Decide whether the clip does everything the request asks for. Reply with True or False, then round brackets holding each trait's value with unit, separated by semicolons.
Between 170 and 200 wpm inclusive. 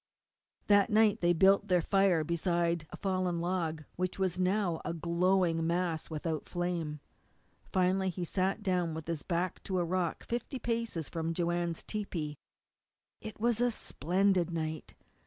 False (155 wpm)